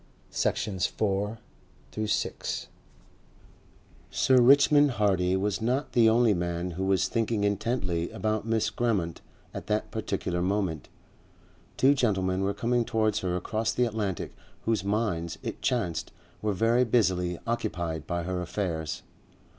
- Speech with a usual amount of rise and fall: Yes, average, 4.3 semitones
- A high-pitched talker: No, low, 105 Hz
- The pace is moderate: No, slow, 125 wpm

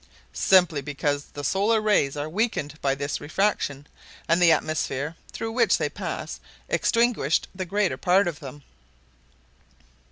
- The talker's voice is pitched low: No, medium, 160 Hz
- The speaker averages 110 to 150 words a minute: Yes, slow, 135 wpm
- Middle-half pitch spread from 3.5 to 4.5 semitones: No, wide, 5.6 semitones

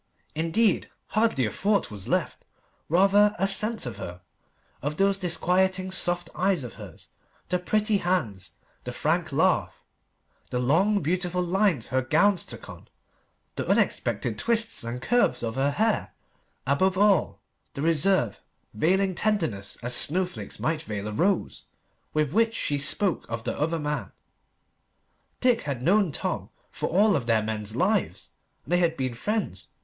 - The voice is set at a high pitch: No, medium, 175 Hz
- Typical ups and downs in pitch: No, wide, 7.3 semitones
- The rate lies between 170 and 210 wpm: No, average, 150 wpm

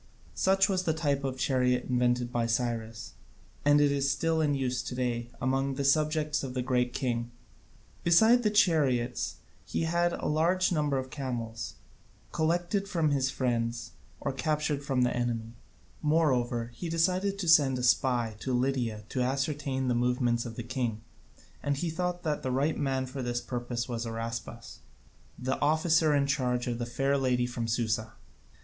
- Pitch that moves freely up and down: No, average, 3.9 semitones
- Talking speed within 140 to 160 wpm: No, average, 170 wpm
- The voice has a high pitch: No, low, 130 Hz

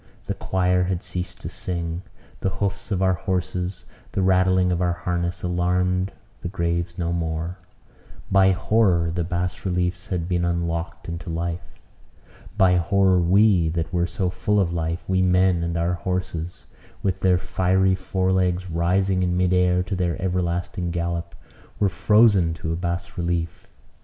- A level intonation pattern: Yes, narrow, 1.4 semitones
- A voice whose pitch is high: No, very low, 90 Hz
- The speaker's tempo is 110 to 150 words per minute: No, average, 160 wpm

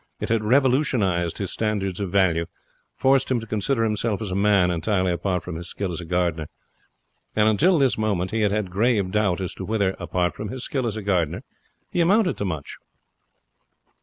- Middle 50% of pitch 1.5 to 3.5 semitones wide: No, average, 3.9 semitones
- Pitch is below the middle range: Yes, low, 100 Hz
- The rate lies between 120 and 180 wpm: No, average, 195 wpm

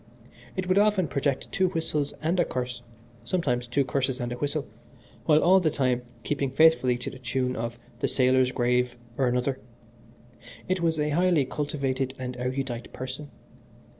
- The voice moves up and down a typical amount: Yes, average, 3.8 semitones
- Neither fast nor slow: Yes, average, 165 wpm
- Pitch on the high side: No, low, 135 Hz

